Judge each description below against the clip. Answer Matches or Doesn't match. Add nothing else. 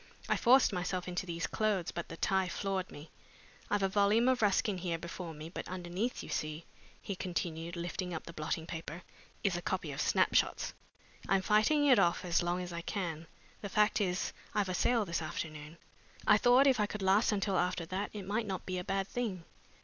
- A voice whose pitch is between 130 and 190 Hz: Matches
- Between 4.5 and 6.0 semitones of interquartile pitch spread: Doesn't match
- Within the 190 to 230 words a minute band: Matches